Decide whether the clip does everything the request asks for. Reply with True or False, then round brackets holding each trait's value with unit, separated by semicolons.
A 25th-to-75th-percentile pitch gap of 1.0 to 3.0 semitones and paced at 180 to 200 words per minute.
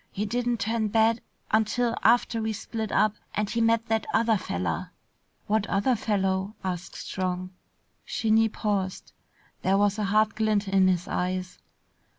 False (2.7 semitones; 150 wpm)